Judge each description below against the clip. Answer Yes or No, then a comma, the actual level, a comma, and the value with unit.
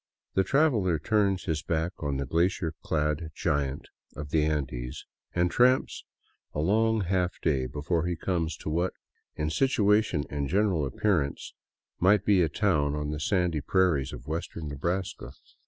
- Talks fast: No, average, 155 wpm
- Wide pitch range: No, average, 4.5 semitones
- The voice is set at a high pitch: No, very low, 85 Hz